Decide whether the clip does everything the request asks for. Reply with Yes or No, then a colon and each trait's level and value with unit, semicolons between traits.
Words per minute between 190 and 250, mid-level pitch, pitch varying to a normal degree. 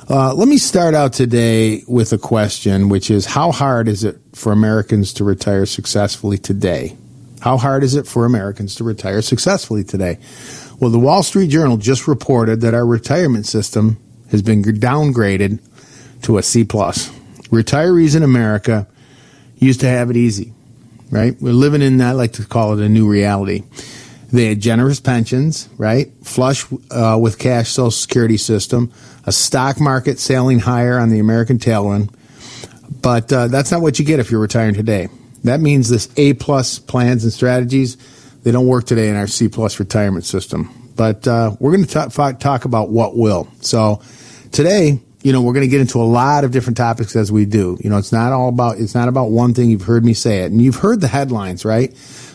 No: average, 195 wpm; low, 120 Hz; average, 3.2 semitones